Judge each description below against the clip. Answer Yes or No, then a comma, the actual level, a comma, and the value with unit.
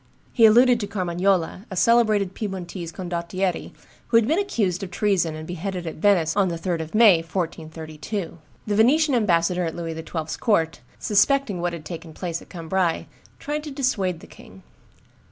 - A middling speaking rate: Yes, average, 170 wpm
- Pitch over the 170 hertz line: Yes, medium, 185 Hz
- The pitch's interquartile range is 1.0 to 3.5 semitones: No, average, 4.2 semitones